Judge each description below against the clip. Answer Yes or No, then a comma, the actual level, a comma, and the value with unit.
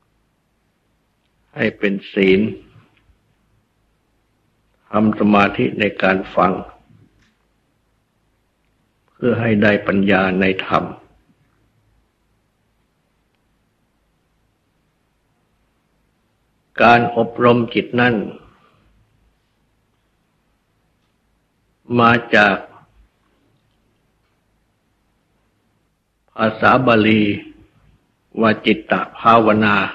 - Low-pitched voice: Yes, low, 110 Hz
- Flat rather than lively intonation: Yes, narrow, 2.3 semitones